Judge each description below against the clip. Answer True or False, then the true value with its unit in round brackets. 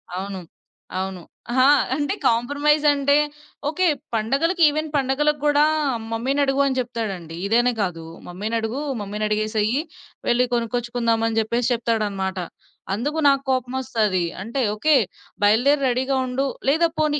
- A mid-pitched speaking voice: False (245 Hz)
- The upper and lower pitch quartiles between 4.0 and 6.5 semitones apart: True (4.6 semitones)